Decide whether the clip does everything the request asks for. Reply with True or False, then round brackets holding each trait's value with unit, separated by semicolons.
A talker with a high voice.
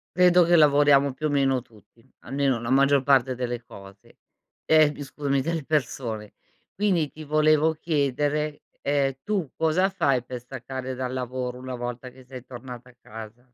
False (135 Hz)